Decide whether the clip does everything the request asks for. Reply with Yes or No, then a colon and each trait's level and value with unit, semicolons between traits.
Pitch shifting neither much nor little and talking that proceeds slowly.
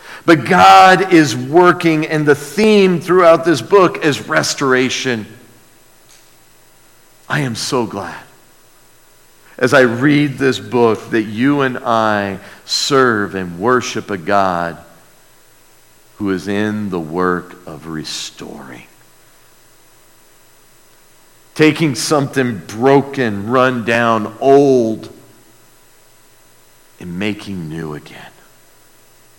No: wide, 6.7 semitones; slow, 95 wpm